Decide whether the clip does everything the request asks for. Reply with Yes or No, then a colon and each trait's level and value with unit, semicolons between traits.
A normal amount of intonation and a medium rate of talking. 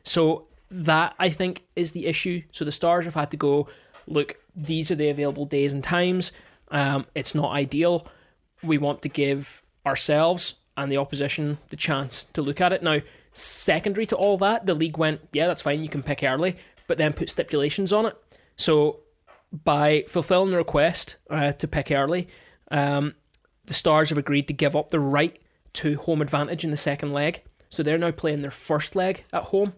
Yes: average, 3.2 semitones; average, 195 wpm